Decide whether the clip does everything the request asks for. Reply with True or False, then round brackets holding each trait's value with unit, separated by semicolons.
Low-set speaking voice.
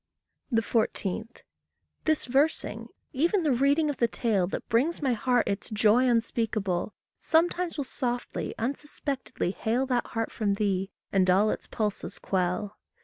False (235 Hz)